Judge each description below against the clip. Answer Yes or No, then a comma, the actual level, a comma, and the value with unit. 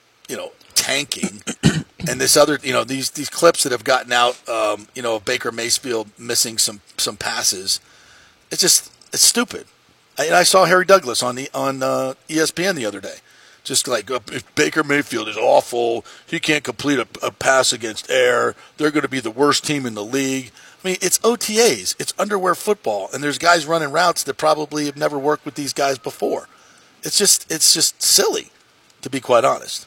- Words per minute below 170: No, average, 195 wpm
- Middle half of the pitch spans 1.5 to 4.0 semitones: No, average, 4.4 semitones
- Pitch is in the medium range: Yes, medium, 145 Hz